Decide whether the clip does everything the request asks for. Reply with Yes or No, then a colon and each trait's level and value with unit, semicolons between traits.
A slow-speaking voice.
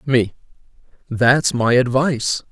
Yes: slow, 95 wpm